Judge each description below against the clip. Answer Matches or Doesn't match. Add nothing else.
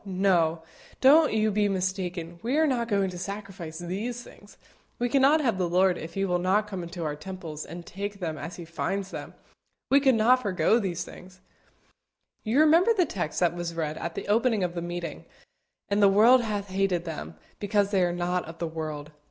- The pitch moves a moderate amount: Matches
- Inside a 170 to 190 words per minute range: Doesn't match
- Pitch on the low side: Doesn't match